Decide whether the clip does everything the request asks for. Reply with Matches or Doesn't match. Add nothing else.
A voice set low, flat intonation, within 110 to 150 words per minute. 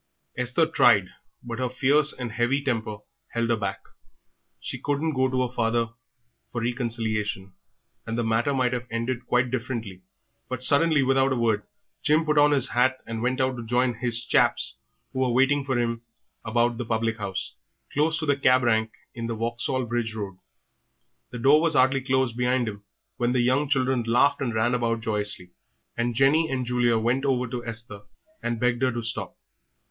Doesn't match